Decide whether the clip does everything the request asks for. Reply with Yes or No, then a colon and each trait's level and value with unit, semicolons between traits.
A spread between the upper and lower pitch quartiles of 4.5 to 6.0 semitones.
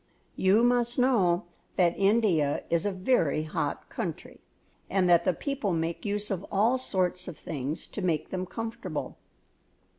Yes: average, 4.8 semitones